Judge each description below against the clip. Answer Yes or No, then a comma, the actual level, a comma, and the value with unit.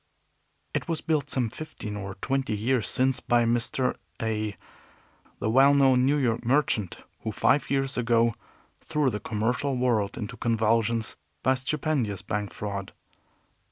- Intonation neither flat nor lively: Yes, average, 3.8 semitones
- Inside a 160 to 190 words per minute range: No, average, 145 wpm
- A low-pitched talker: Yes, low, 120 Hz